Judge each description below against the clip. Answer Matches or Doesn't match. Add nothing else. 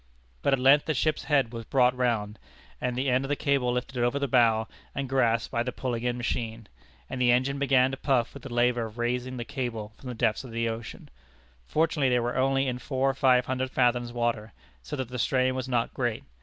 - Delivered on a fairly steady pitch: Matches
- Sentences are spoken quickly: Matches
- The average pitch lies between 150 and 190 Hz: Doesn't match